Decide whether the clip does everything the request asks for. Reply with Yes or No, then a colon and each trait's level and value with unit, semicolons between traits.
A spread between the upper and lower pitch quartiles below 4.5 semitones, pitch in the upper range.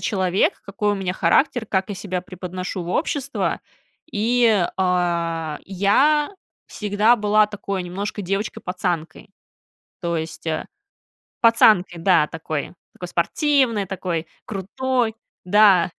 Yes: average, 3.2 semitones; high, 195 Hz